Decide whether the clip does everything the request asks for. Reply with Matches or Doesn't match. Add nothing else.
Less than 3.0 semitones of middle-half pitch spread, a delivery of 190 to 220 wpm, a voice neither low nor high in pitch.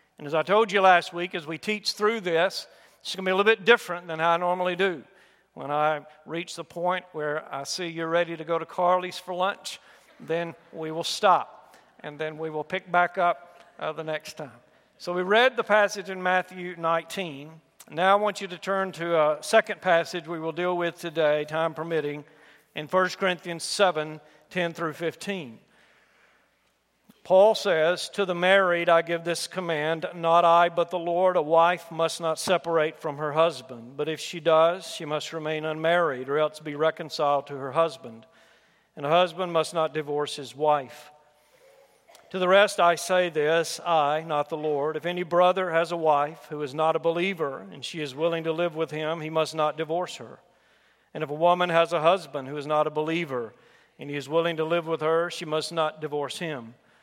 Matches